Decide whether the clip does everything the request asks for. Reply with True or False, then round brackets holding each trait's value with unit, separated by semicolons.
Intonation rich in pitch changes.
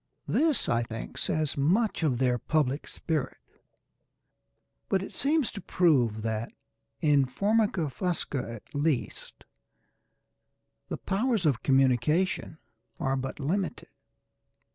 True (6.7 semitones)